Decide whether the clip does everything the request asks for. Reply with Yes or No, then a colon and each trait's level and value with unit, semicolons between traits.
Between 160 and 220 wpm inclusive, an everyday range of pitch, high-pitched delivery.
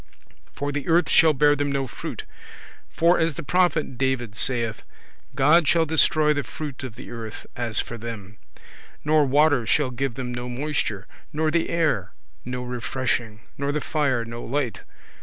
No: average, 165 wpm; average, 4.0 semitones; low, 135 Hz